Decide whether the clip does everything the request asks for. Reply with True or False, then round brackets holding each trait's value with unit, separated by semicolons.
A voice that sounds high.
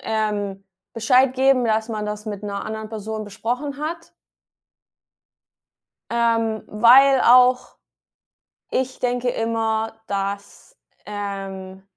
True (225 Hz)